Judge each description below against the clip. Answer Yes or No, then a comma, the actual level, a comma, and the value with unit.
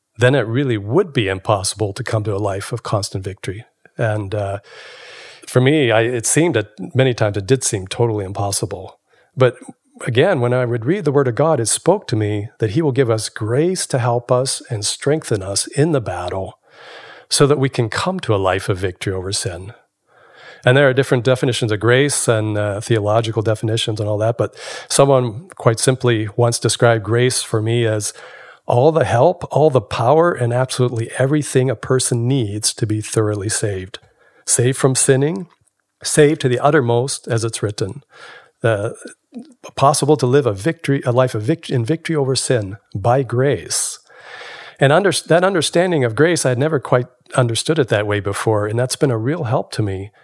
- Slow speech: No, average, 190 wpm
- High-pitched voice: No, low, 120 Hz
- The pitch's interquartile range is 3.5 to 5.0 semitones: Yes, average, 4.2 semitones